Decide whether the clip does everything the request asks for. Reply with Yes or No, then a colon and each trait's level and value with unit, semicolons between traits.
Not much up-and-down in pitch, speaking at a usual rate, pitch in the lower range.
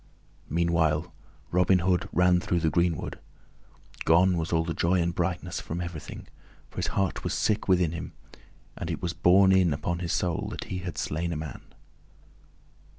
Yes: narrow, 1.6 semitones; average, 170 wpm; very low, 85 Hz